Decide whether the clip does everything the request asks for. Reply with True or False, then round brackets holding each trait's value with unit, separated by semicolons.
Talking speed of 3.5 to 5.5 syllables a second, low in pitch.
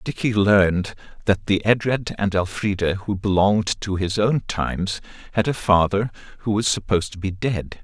True (5.0 syllables/s; 100 Hz)